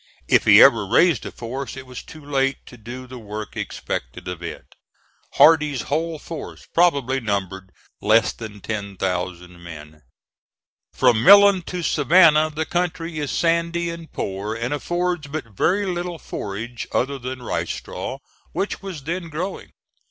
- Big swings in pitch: Yes, wide, 7.6 semitones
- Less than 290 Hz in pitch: Yes, low, 135 Hz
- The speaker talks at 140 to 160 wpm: Yes, average, 150 wpm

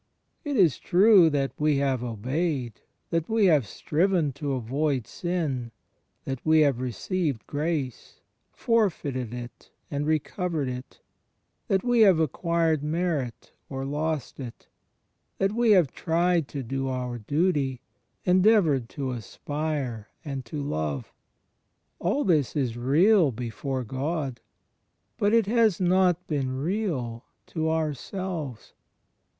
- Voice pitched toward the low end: No, medium, 150 Hz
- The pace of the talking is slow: Yes, slow, 120 wpm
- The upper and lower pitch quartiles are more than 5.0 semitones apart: Yes, wide, 5.4 semitones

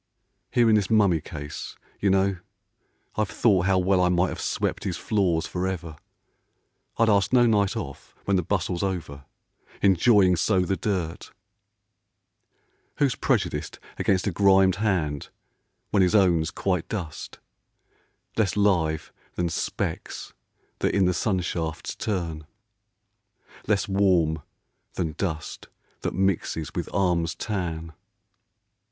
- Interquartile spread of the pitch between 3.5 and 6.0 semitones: No, average, 3.0 semitones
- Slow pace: Yes, slow, 130 wpm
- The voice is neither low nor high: No, very low, 95 Hz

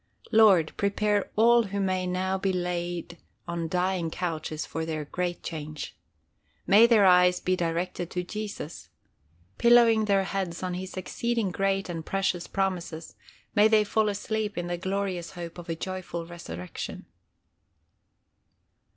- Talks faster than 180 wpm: No, average, 140 wpm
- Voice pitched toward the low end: No, medium, 185 Hz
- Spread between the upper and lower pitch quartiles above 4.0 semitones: No, average, 2.7 semitones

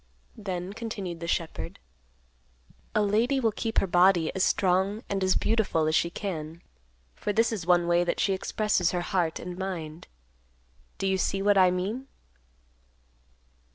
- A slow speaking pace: No, average, 155 wpm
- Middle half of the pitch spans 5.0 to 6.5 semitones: No, average, 3.0 semitones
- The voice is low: No, high, 190 Hz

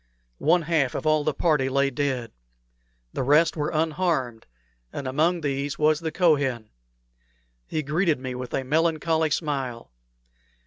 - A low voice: No, medium, 150 Hz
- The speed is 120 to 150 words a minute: Yes, average, 140 wpm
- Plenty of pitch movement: No, average, 3.2 semitones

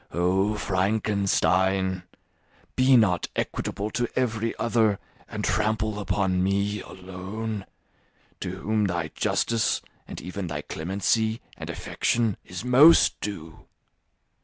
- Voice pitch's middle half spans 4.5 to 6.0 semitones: No, average, 2.9 semitones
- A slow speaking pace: Yes, slow, 110 wpm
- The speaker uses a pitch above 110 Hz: No, low, 100 Hz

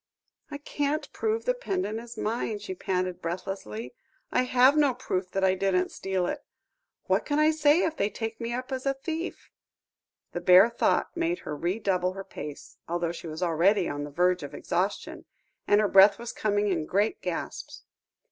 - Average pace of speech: Yes, average, 185 wpm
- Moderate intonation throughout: No, wide, 6.6 semitones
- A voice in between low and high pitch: No, high, 205 Hz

